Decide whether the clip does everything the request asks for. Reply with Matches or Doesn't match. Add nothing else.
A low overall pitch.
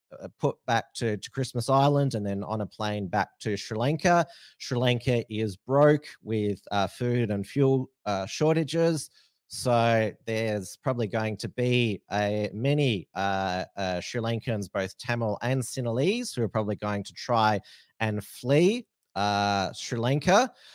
Matches